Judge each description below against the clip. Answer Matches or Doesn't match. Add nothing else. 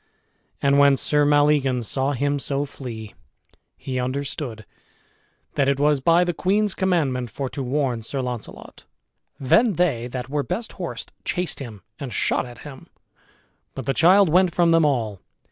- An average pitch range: Matches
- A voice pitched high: Doesn't match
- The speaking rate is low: Doesn't match